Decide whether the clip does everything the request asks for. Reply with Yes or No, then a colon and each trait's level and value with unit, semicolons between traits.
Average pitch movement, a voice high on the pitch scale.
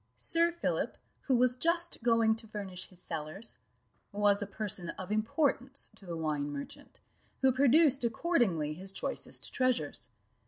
No: wide, 5.9 semitones; high, 220 Hz